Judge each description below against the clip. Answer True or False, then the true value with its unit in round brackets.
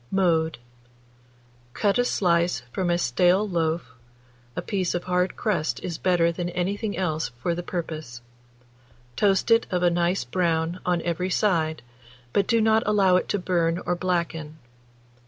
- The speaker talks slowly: False (155 wpm)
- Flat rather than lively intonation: True (2.3 semitones)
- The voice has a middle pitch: True (175 Hz)